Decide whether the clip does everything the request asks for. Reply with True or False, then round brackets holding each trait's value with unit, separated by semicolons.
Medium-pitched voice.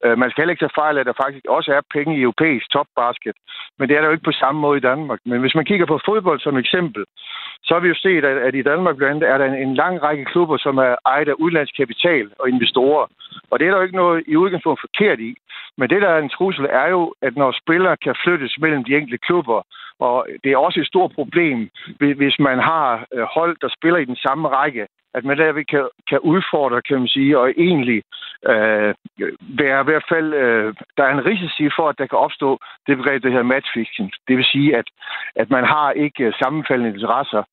True (145 Hz)